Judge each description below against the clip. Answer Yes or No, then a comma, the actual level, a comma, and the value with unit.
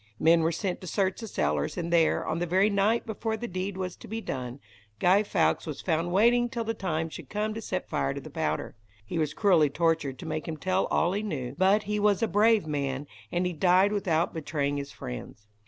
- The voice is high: No, medium, 180 Hz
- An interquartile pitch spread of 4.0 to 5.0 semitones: Yes, average, 4.7 semitones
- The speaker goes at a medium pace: No, fast, 230 wpm